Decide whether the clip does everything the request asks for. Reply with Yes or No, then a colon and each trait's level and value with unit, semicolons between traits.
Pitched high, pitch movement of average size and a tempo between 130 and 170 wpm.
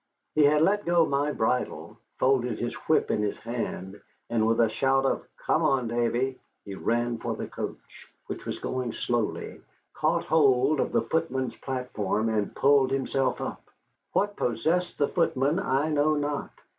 No: low, 135 Hz; average, 4.0 semitones; average, 165 wpm